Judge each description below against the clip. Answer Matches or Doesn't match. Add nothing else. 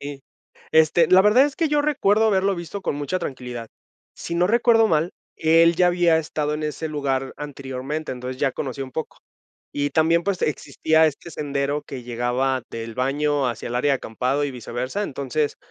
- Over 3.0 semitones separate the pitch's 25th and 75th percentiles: Matches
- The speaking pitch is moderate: Matches